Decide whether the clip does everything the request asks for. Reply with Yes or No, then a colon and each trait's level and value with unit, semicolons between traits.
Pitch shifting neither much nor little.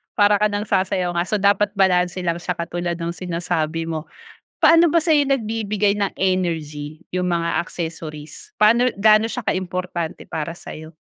Yes: average, 3.6 semitones